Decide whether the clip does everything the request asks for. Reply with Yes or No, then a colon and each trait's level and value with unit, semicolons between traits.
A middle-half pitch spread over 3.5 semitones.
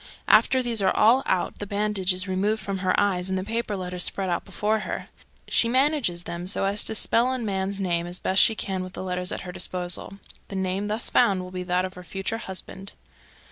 No: narrow, 2.5 semitones